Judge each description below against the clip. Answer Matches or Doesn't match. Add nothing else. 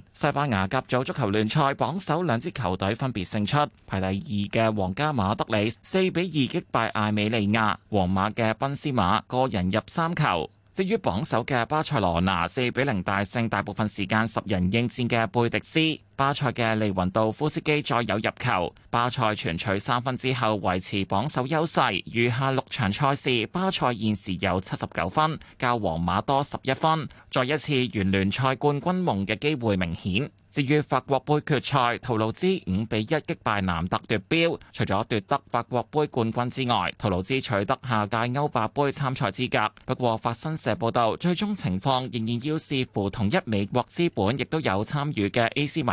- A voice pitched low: Matches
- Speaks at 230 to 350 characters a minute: Matches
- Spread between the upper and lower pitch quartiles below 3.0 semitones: Doesn't match